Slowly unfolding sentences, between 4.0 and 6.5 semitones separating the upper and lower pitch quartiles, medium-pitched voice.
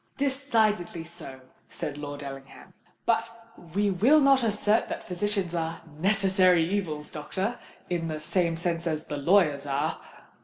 Yes: slow, 130 wpm; average, 4.9 semitones; medium, 175 Hz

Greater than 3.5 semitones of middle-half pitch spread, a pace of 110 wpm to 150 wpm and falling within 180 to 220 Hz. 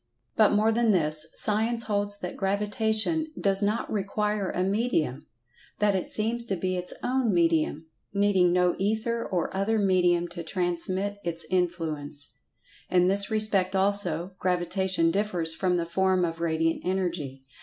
No: average, 3.2 semitones; average, 145 wpm; high, 190 Hz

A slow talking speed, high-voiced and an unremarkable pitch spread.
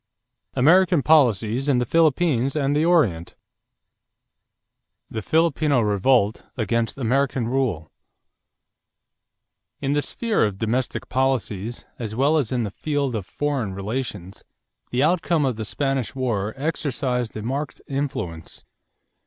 No: slow, 120 wpm; low, 130 Hz; average, 4.7 semitones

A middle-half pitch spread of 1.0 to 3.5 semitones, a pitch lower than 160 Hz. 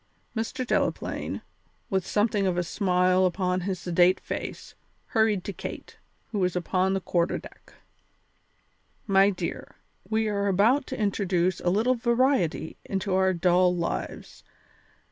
No: narrow, 2.6 semitones; high, 190 Hz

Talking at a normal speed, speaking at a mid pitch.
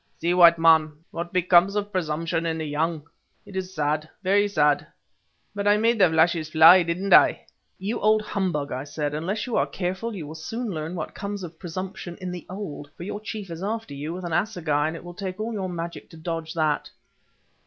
No: fast, 210 wpm; medium, 175 Hz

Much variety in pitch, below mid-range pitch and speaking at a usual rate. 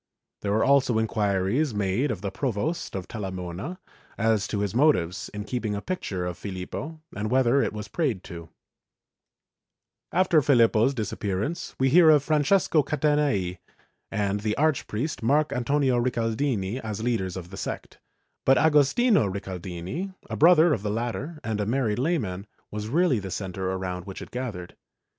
Yes: wide, 6.7 semitones; low, 115 Hz; average, 160 wpm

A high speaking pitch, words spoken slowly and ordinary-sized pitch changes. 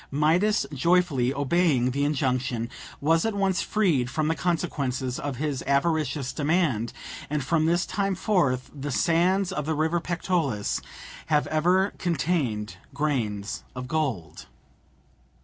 No: medium, 150 Hz; slow, 130 wpm; average, 4.9 semitones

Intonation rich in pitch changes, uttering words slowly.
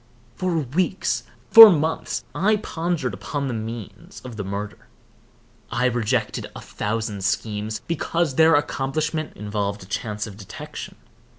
Yes: wide, 7.5 semitones; slow, 130 wpm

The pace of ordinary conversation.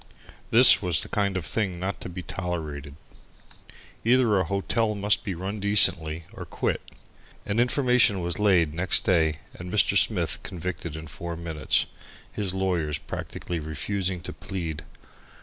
Yes: average, 150 wpm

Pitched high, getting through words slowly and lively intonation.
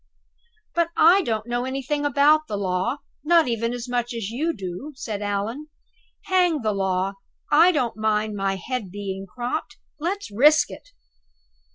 No: high, 240 Hz; average, 155 wpm; wide, 6.7 semitones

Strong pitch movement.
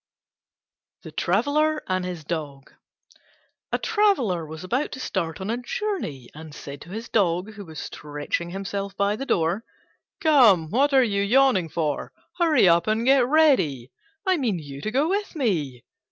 Yes: wide, 8.8 semitones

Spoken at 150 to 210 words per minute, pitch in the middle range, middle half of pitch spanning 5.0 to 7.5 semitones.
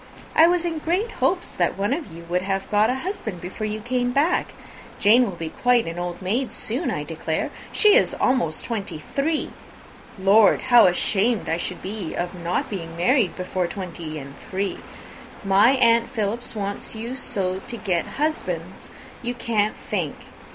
No: average, 175 wpm; high, 210 Hz; average, 5.3 semitones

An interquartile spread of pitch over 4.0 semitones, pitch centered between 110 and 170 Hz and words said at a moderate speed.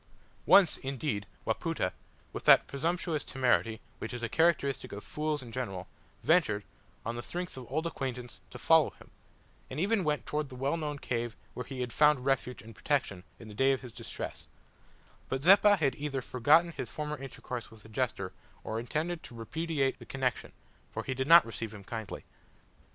Yes: average, 4.5 semitones; low, 135 Hz; average, 185 wpm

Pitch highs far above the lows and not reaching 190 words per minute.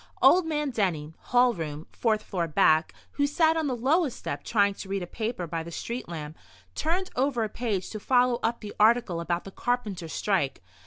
No: wide, 6.4 semitones; average, 200 wpm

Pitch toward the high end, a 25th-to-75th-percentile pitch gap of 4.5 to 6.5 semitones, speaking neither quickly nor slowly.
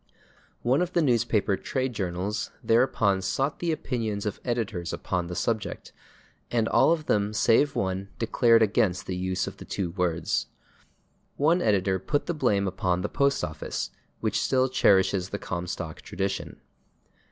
No: low, 105 Hz; average, 5.1 semitones; average, 150 wpm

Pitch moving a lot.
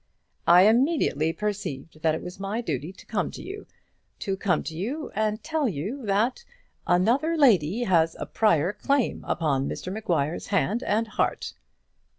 Yes: wide, 6.3 semitones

